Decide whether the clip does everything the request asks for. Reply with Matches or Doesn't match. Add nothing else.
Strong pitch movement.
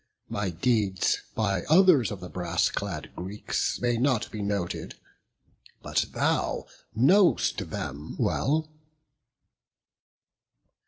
Matches